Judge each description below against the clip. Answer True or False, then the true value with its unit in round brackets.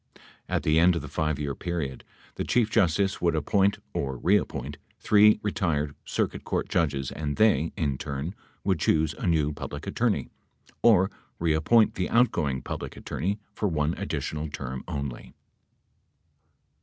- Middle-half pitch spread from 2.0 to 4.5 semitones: False (4.9 semitones)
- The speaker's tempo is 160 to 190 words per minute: False (145 wpm)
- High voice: False (80 Hz)